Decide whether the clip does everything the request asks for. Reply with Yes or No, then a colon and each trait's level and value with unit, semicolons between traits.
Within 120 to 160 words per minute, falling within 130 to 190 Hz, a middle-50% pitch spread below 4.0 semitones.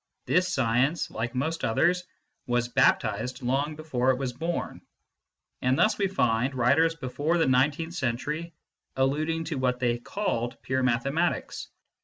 No: average, 140 wpm; low, 135 Hz; average, 4.7 semitones